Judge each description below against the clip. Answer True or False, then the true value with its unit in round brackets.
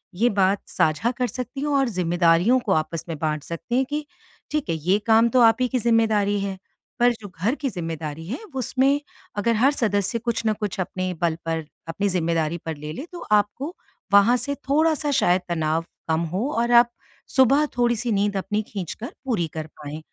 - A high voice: True (205 Hz)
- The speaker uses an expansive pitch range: True (6.4 semitones)